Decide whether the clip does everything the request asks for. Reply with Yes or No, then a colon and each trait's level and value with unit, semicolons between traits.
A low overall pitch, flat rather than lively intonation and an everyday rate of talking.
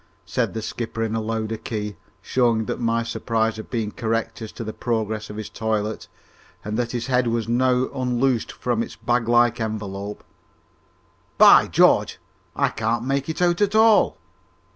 Yes: low, 115 Hz; narrow, 2.0 semitones; average, 170 wpm